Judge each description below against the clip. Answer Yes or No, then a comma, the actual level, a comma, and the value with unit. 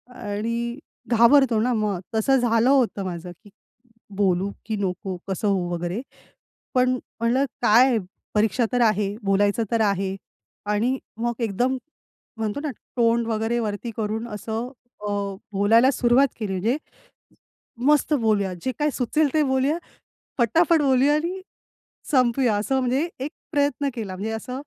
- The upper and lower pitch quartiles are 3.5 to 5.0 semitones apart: Yes, average, 4.1 semitones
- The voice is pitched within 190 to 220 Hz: No, high, 230 Hz